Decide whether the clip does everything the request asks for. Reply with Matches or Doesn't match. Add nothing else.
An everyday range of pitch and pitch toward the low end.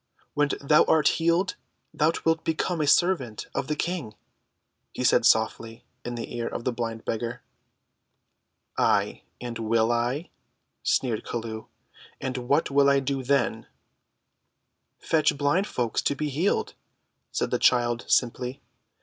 Matches